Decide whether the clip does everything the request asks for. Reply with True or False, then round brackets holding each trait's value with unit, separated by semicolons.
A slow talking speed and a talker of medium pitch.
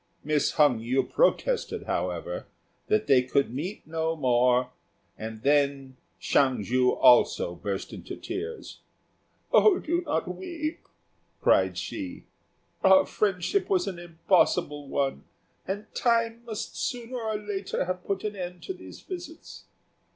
True (130 wpm; 180 Hz)